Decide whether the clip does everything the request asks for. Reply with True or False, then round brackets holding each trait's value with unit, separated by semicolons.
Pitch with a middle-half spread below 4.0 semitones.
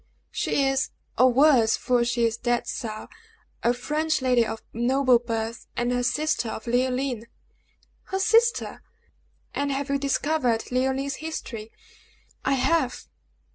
True (2.8 semitones)